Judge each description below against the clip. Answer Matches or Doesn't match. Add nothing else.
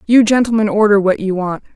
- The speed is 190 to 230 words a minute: Matches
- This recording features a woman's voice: Matches